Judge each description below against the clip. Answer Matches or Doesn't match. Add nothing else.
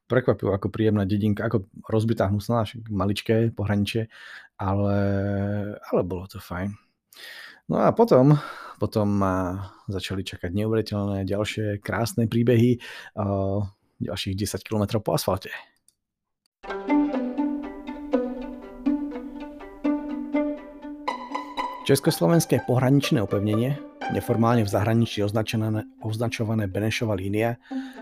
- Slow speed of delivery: Matches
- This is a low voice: Matches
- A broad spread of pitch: Matches